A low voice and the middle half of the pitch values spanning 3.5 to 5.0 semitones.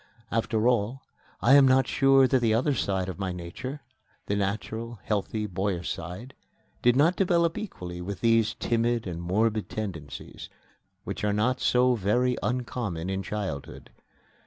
Yes: low, 110 Hz; average, 4.6 semitones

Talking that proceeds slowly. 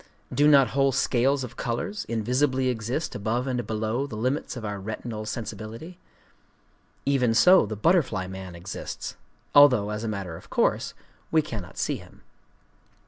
No: average, 145 wpm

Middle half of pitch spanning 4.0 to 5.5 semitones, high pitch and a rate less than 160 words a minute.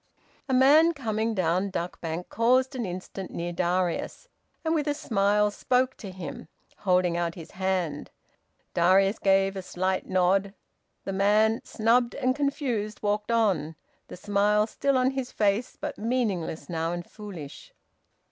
Yes: average, 4.5 semitones; high, 200 Hz; average, 145 wpm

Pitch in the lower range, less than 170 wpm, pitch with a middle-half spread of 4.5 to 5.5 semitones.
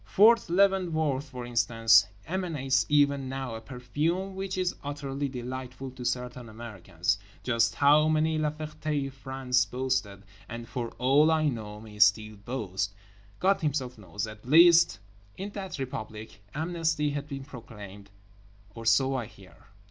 Yes: low, 130 Hz; average, 140 wpm; average, 5.2 semitones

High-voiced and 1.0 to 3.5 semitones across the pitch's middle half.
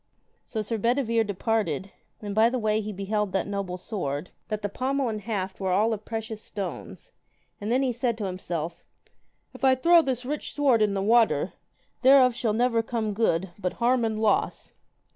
Yes: high, 220 Hz; average, 3.2 semitones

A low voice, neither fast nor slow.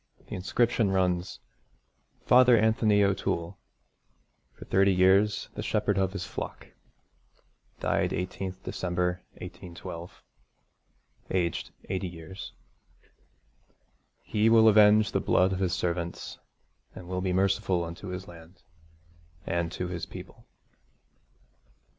No: very low, 95 Hz; slow, 110 wpm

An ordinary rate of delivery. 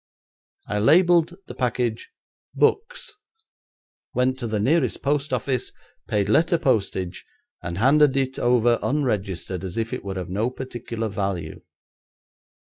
No: slow, 130 wpm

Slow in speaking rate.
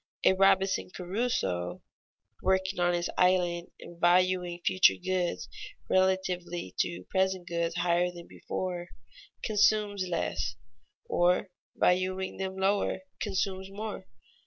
Yes: slow, 110 wpm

